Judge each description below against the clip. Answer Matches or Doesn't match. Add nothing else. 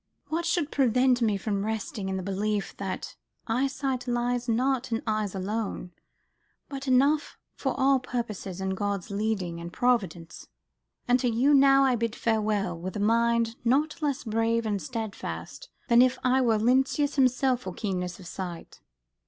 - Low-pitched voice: Doesn't match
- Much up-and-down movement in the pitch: Doesn't match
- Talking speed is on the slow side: Doesn't match